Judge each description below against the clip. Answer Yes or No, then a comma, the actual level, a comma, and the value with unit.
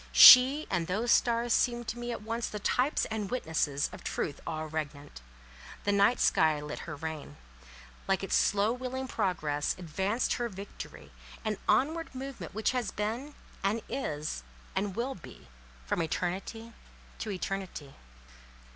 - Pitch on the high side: Yes, high, 205 Hz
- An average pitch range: No, wide, 6.8 semitones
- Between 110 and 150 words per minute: Yes, average, 145 wpm